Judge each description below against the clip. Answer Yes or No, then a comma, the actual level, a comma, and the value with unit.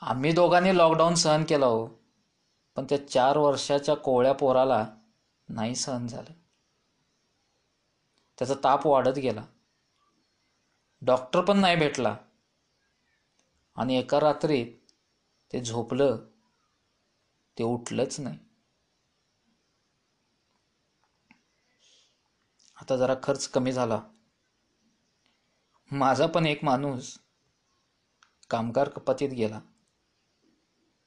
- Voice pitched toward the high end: No, low, 135 Hz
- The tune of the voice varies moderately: Yes, average, 3.0 semitones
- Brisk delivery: No, average, 85 wpm